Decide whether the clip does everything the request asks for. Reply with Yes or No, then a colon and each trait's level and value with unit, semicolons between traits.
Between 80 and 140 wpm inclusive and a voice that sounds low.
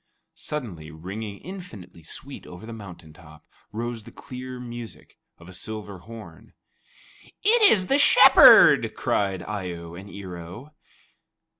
Yes: slow, 135 wpm; low, 105 Hz